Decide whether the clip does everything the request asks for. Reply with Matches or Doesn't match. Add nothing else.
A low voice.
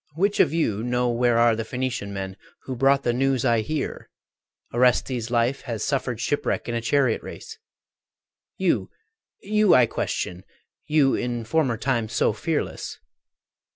Matches